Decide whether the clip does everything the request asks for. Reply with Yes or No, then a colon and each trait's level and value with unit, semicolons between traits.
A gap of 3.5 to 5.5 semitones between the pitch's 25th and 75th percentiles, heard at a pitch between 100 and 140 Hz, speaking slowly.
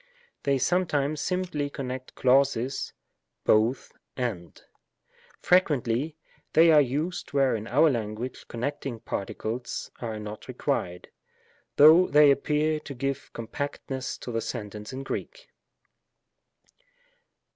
Yes: average, 4.3 semitones; low, 135 Hz; slow, 115 wpm